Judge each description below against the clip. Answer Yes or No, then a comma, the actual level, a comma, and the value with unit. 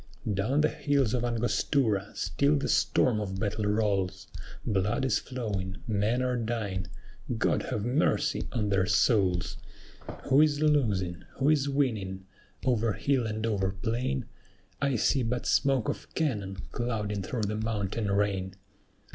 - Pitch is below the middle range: Yes, low, 110 Hz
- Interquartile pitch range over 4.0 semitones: Yes, average, 4.4 semitones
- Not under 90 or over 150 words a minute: Yes, average, 140 wpm